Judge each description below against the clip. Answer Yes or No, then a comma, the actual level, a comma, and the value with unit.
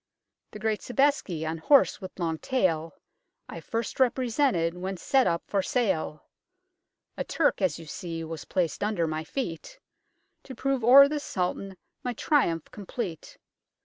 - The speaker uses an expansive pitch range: Yes, wide, 7.3 semitones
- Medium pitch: No, high, 195 Hz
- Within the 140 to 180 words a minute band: Yes, average, 145 wpm